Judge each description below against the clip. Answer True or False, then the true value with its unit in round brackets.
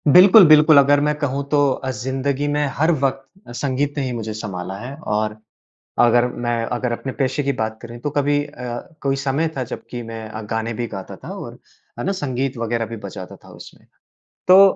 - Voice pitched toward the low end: True (130 Hz)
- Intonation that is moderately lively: True (3.8 semitones)